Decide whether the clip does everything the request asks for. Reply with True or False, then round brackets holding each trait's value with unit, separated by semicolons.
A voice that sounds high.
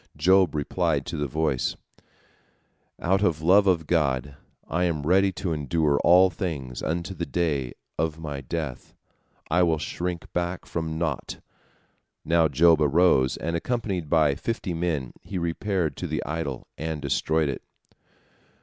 False (80 Hz)